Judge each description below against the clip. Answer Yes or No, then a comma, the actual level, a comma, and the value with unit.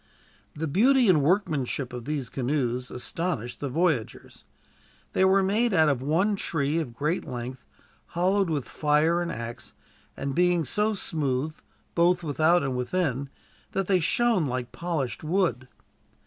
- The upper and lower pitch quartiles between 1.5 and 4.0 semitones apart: No, average, 5.3 semitones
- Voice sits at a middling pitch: Yes, medium, 155 Hz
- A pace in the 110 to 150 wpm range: Yes, average, 145 wpm